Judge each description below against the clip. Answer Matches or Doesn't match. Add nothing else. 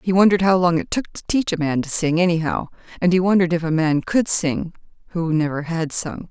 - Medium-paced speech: Doesn't match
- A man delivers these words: Doesn't match